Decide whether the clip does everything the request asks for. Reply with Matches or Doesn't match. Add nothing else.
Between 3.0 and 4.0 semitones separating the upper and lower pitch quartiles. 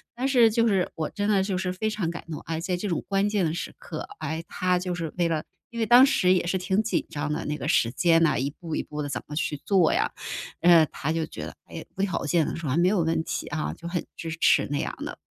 Matches